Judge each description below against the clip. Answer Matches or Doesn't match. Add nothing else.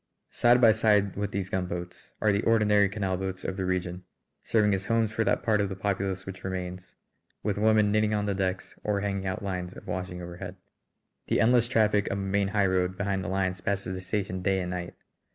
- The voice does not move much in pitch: Matches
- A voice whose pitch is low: Matches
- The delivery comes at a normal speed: Doesn't match